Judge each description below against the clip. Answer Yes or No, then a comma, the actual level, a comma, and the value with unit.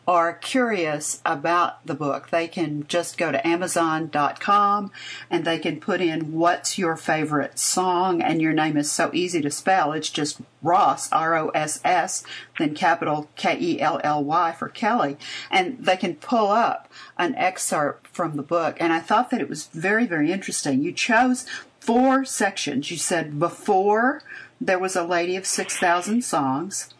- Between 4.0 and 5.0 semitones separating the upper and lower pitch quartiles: Yes, average, 4.3 semitones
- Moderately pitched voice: Yes, medium, 175 Hz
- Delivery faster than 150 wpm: Yes, average, 170 wpm